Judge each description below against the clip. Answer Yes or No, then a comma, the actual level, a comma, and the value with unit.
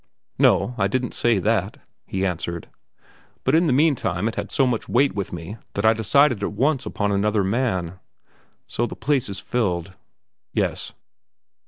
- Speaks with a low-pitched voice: Yes, low, 110 Hz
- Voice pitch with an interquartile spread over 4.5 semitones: Yes, average, 4.9 semitones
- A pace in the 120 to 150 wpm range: No, average, 165 wpm